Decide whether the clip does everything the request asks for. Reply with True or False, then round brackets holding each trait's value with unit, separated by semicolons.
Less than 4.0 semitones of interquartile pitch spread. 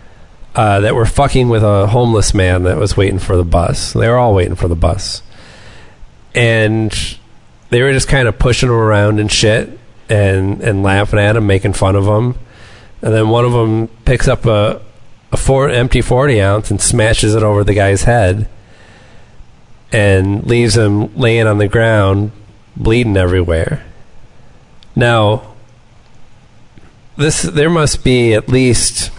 True (2.9 semitones)